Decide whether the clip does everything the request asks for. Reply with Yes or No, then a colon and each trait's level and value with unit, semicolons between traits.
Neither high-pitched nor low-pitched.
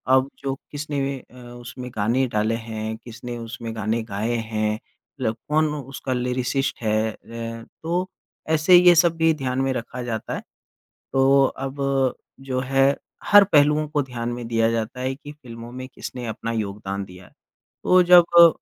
No: low, 125 Hz